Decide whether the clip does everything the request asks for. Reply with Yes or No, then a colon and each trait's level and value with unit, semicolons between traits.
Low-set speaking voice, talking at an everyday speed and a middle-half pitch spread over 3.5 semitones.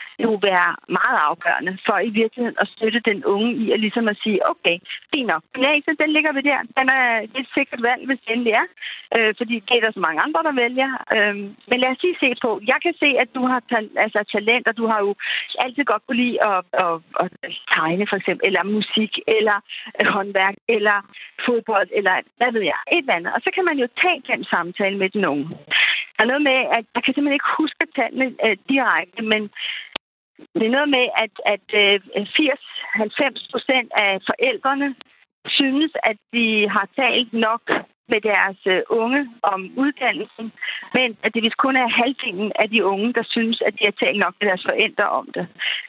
No: high, 230 Hz; average, 195 wpm; average, 4.0 semitones